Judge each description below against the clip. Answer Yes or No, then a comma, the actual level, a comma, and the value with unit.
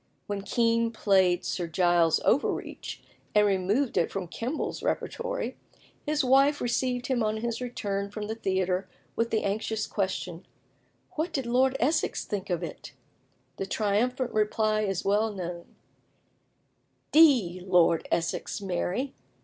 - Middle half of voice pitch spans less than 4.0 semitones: No, average, 4.7 semitones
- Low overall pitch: No, high, 210 Hz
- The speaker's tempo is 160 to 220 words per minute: No, slow, 135 wpm